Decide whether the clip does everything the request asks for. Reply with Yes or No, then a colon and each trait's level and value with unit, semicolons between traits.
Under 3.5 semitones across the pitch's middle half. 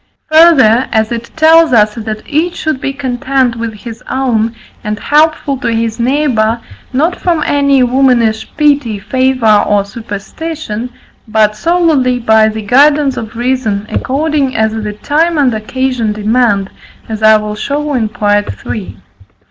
No: average, 4.6 semitones